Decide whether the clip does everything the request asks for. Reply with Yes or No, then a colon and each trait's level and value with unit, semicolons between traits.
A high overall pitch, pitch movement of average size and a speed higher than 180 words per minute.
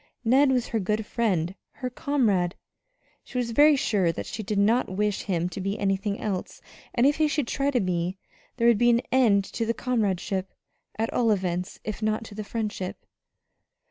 Yes: high, 215 Hz; average, 3.8 semitones; average, 190 wpm